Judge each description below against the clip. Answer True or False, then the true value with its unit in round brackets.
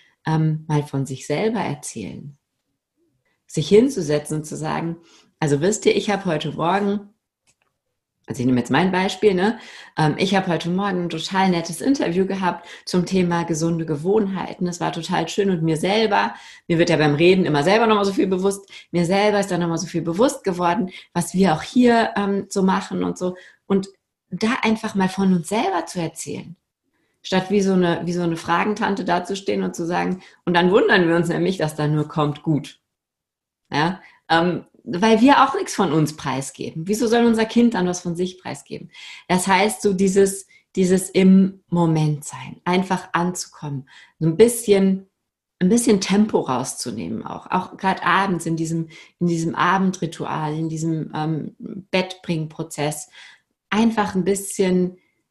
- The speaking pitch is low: False (180 Hz)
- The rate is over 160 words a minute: True (170 wpm)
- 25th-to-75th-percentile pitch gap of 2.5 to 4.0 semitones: True (3.3 semitones)